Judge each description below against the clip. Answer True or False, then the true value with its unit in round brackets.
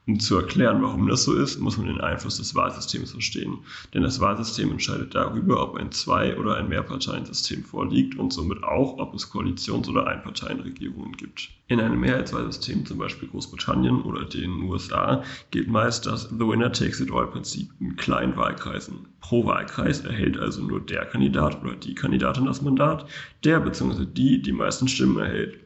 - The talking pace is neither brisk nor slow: True (175 wpm)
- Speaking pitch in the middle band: False (100 Hz)